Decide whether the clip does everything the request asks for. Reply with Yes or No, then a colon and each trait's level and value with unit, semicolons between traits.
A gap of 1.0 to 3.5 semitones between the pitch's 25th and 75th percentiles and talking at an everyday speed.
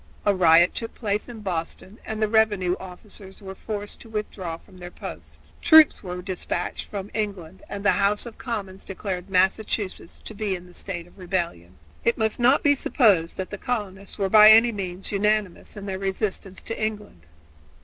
Yes: average, 3.0 semitones; average, 180 wpm